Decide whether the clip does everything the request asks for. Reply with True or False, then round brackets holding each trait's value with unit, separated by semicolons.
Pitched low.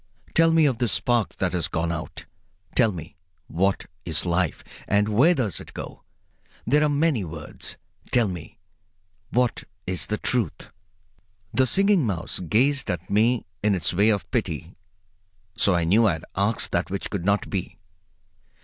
True (100 Hz)